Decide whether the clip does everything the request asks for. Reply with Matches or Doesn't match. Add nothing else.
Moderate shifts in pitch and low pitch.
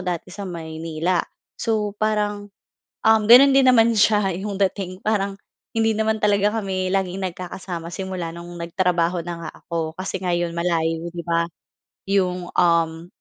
Doesn't match